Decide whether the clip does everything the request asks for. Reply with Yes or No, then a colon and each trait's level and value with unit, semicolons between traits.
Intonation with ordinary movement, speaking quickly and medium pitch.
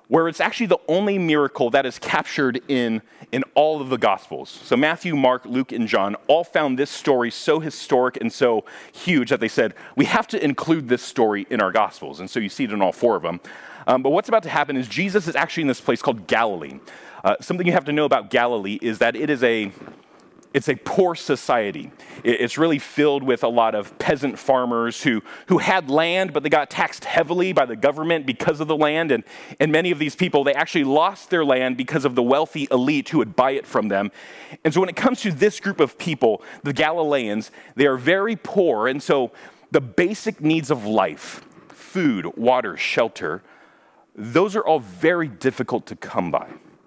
Yes: average, 4.7 semitones; fast, 210 wpm; medium, 150 Hz